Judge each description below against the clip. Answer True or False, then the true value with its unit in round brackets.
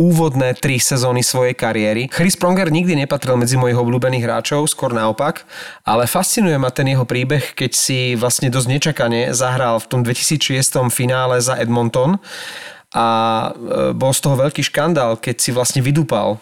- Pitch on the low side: True (130 Hz)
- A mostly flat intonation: False (3.0 semitones)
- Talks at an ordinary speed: True (155 wpm)